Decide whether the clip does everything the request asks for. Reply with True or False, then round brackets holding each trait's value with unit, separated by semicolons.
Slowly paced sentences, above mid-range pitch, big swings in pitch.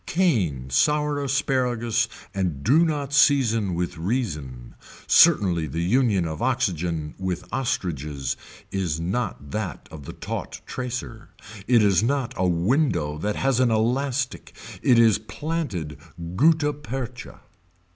False (125 wpm; 110 Hz; 7.8 semitones)